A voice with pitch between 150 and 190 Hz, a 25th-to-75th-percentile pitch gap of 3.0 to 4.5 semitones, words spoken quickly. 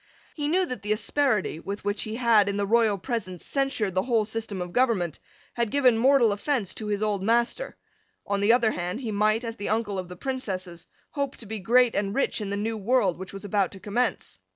No: high, 215 Hz; average, 3.4 semitones; fast, 225 wpm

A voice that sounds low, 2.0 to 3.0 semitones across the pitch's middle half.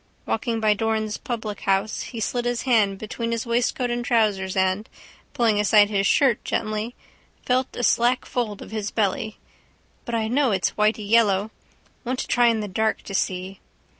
No: high, 220 Hz; narrow, 2.5 semitones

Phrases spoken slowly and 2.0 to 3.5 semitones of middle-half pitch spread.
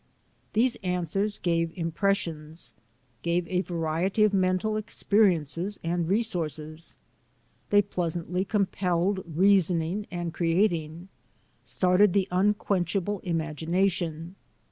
Yes: slow, 100 wpm; average, 2.9 semitones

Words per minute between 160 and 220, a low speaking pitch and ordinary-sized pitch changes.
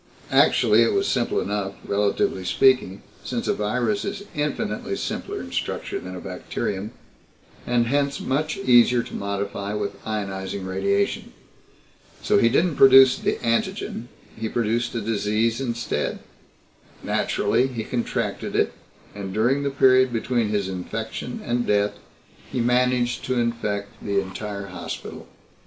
No: slow, 135 wpm; low, 115 Hz; average, 3.9 semitones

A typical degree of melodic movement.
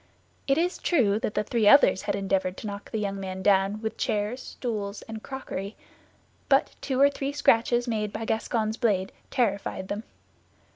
Yes: average, 3.5 semitones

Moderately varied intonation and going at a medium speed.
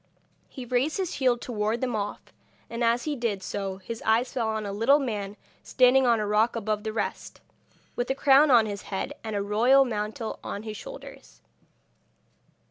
Yes: average, 3.3 semitones; average, 190 wpm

